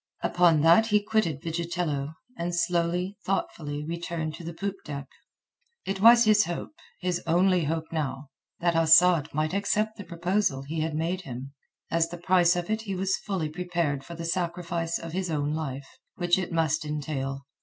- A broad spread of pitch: No, average, 2.8 semitones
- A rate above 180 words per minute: No, average, 165 wpm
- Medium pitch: Yes, medium, 170 Hz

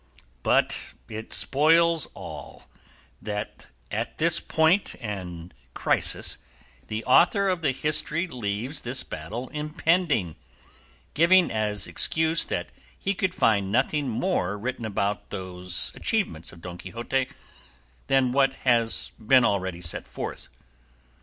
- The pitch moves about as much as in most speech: No, wide, 7.7 semitones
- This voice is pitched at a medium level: No, low, 125 Hz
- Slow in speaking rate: Yes, slow, 120 wpm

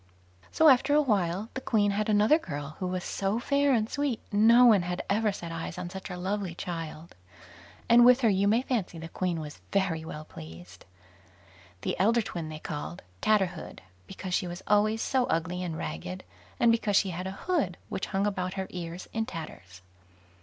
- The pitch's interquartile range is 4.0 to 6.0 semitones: Yes, average, 4.5 semitones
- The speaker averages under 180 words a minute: No, average, 190 wpm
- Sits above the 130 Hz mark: Yes, high, 190 Hz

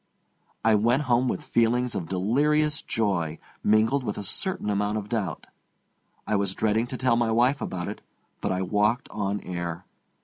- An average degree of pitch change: Yes, average, 3.6 semitones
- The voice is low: Yes, low, 110 Hz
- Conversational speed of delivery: Yes, average, 170 wpm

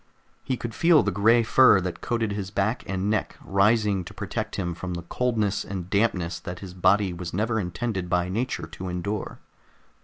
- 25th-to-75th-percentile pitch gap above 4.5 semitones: No, average, 3.6 semitones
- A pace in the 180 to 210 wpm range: Yes, average, 185 wpm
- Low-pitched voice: Yes, low, 100 Hz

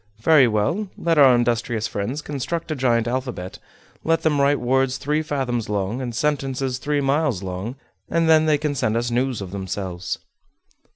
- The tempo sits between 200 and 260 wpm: No, average, 170 wpm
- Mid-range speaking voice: No, low, 130 Hz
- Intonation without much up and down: No, average, 4.5 semitones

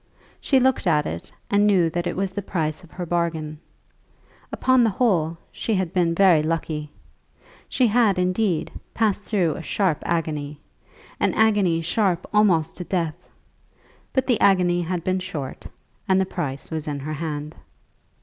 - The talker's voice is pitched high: No, medium, 175 Hz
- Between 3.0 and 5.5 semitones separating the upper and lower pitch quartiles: Yes, average, 3.8 semitones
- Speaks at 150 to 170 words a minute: Yes, average, 160 wpm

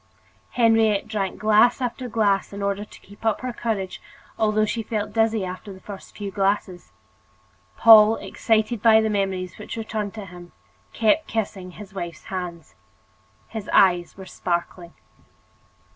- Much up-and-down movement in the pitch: No, average, 2.7 semitones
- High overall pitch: Yes, high, 210 Hz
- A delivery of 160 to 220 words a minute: No, average, 145 wpm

